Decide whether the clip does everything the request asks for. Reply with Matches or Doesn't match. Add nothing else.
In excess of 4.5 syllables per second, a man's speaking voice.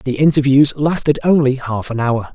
Matches